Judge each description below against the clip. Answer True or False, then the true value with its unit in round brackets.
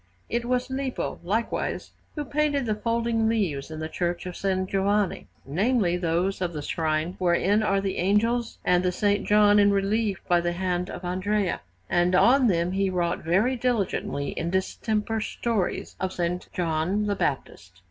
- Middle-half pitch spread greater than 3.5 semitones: True (4.0 semitones)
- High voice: True (195 Hz)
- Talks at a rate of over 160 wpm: True (170 wpm)